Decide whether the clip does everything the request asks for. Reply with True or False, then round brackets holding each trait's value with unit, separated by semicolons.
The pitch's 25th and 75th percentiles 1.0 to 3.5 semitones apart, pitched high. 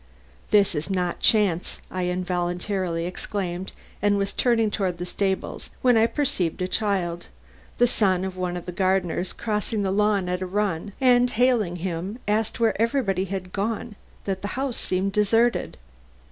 True (3.0 semitones; 195 Hz)